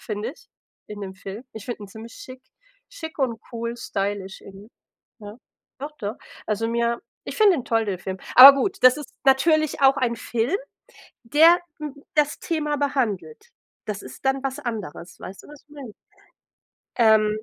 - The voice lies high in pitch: Yes, high, 235 Hz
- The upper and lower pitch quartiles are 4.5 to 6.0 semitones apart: Yes, average, 5.1 semitones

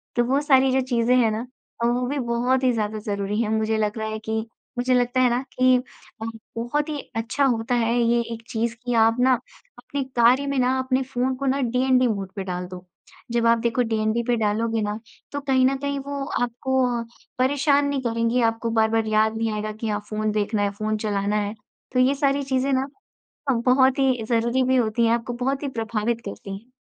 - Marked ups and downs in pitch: No, average, 2.9 semitones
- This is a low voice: No, high, 235 Hz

